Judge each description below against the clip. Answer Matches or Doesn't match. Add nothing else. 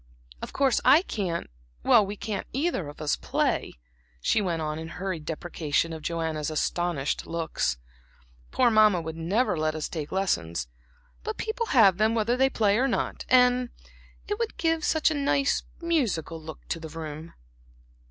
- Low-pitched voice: Doesn't match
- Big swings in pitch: Matches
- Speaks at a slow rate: Doesn't match